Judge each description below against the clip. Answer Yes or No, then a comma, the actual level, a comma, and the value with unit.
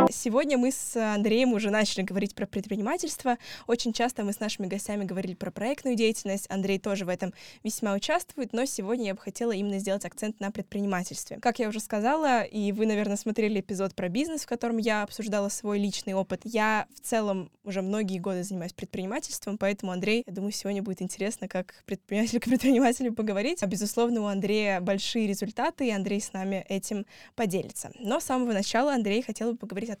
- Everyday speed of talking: No, fast, 190 wpm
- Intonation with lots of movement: No, average, 2.9 semitones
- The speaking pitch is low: No, high, 210 Hz